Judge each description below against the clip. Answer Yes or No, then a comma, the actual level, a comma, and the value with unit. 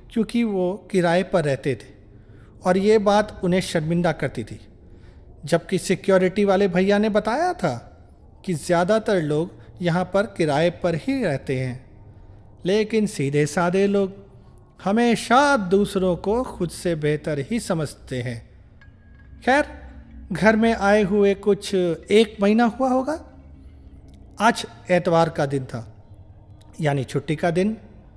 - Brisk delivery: No, average, 130 wpm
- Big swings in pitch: Yes, wide, 9.0 semitones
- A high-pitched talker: No, medium, 175 Hz